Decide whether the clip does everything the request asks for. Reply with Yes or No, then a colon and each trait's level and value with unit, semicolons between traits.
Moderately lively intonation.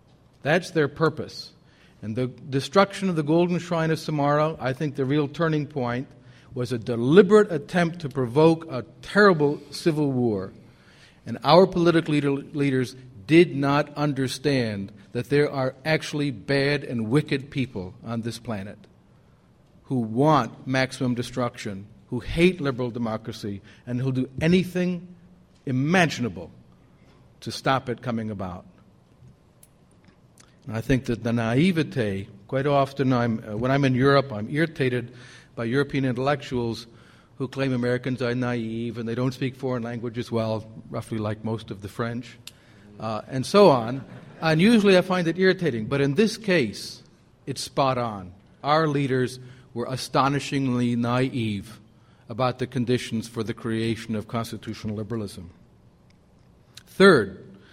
Yes: average, 3.9 semitones